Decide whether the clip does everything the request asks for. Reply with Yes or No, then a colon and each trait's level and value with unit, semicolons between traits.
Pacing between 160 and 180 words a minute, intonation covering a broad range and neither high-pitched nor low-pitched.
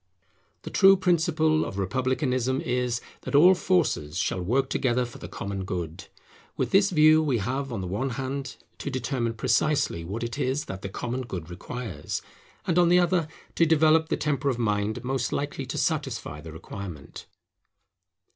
No: average, 170 wpm; wide, 7.1 semitones; low, 130 Hz